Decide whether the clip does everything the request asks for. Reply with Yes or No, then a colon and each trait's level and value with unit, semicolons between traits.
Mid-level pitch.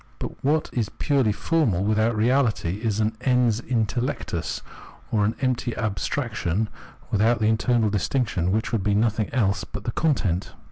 No: low, 110 Hz